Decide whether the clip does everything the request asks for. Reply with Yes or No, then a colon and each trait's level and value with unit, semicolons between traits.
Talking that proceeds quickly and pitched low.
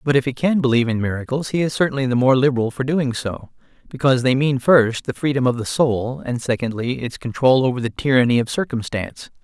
Yes: fast, 215 wpm; low, 130 Hz